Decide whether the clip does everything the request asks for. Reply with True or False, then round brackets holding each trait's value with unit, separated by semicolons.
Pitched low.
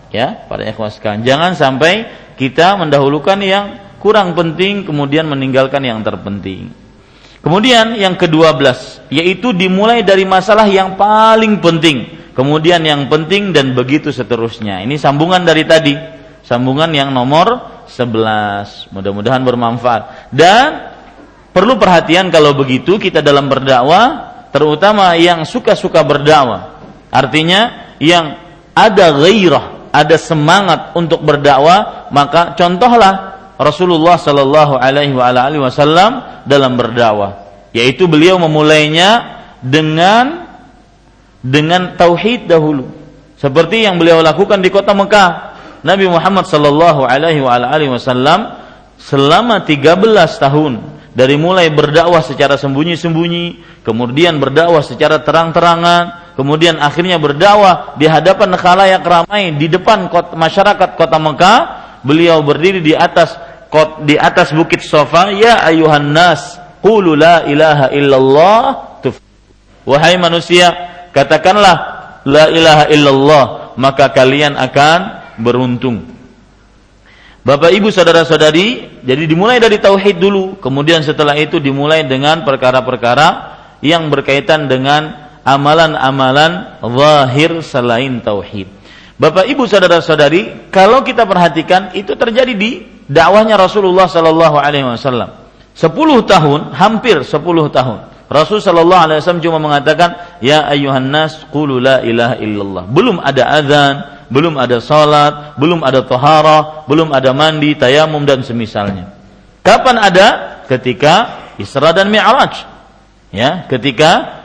False (155 Hz)